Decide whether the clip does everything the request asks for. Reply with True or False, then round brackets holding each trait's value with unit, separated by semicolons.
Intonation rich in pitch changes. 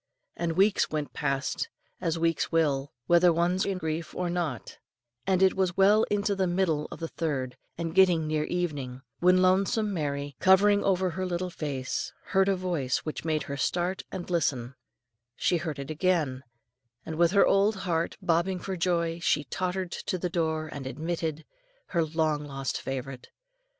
False (3.4 semitones)